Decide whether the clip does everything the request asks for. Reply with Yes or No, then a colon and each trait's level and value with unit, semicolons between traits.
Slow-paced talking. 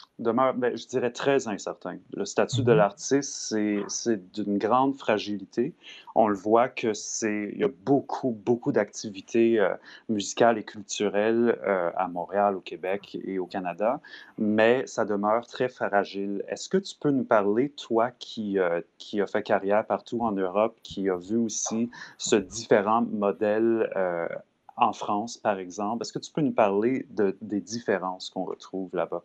No: average, 165 wpm